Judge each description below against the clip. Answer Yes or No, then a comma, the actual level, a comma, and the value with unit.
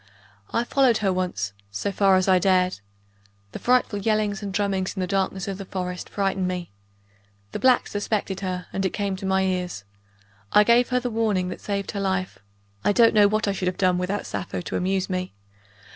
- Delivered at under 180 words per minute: No, fast, 205 wpm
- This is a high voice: Yes, high, 195 Hz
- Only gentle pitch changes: Yes, narrow, 2.0 semitones